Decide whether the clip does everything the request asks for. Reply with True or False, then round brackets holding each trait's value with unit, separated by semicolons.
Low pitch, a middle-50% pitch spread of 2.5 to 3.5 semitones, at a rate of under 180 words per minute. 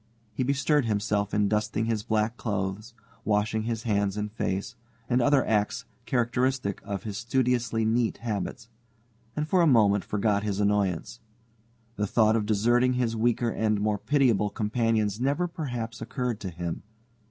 True (110 Hz; 2.8 semitones; 155 wpm)